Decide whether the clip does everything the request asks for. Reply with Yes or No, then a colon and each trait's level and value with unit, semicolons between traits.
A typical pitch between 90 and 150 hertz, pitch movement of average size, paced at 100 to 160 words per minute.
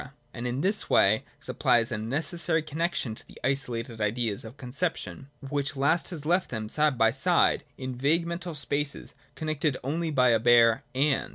No: low, 135 Hz; average, 4.8 semitones; average, 180 wpm